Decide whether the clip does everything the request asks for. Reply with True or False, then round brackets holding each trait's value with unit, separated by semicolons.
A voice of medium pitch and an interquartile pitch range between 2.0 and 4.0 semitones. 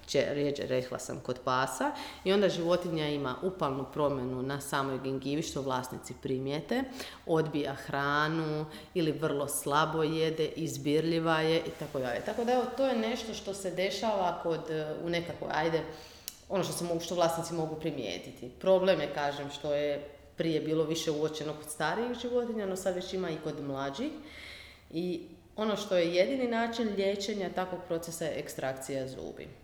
False (160 Hz; 4.4 semitones)